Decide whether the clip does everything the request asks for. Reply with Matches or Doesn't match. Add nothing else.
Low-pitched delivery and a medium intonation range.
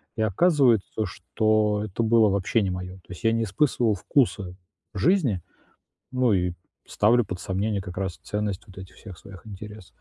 Matches